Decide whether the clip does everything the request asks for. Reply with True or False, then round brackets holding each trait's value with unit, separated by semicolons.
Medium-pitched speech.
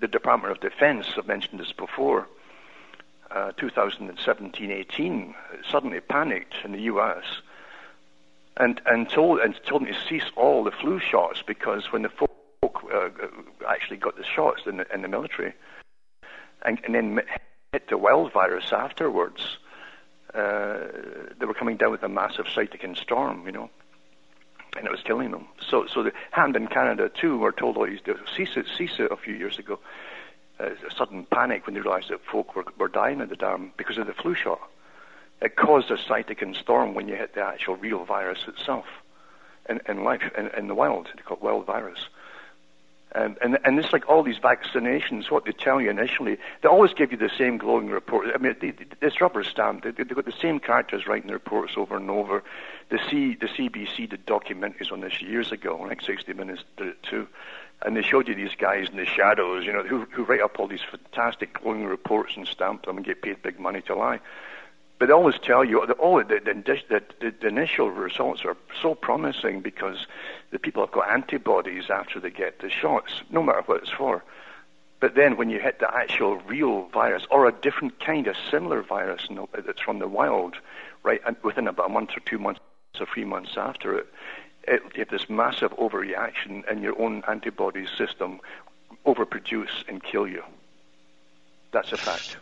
True (165 Hz)